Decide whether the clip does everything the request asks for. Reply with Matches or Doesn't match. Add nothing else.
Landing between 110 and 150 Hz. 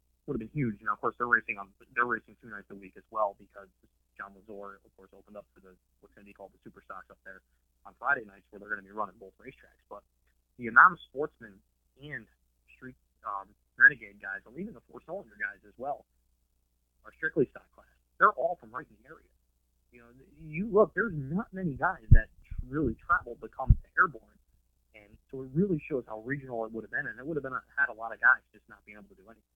Doesn't match